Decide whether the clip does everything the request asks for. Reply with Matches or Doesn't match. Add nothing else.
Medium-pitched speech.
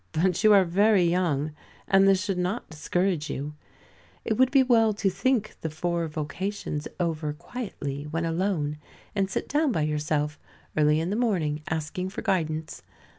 Matches